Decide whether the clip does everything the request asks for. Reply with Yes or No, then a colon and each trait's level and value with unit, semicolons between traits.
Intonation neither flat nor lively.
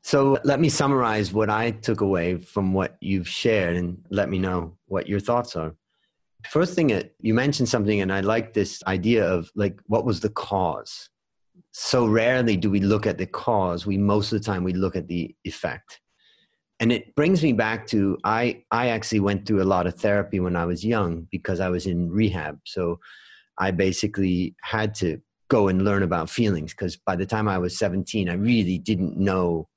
Yes: average, 3.3 semitones